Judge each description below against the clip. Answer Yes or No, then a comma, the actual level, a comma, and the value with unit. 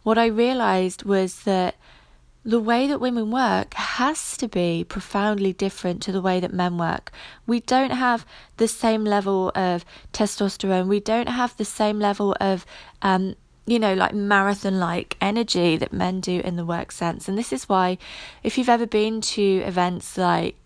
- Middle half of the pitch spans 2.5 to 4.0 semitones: Yes, average, 3.5 semitones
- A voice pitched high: Yes, high, 200 Hz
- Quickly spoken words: No, average, 175 wpm